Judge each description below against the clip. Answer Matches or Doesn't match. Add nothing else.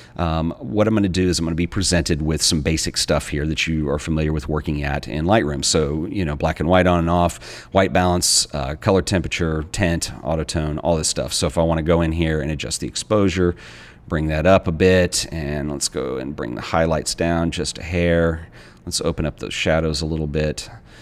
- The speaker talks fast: Matches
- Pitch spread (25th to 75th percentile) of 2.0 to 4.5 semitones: Matches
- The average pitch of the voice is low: Matches